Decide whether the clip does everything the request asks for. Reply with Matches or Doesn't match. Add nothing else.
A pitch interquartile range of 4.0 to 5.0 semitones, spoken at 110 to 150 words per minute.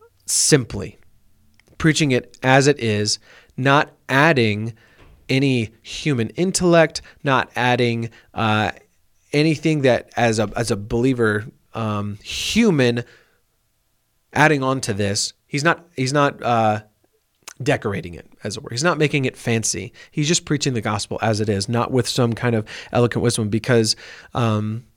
Matches